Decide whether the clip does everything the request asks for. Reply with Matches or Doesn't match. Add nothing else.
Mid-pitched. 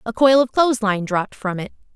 Doesn't match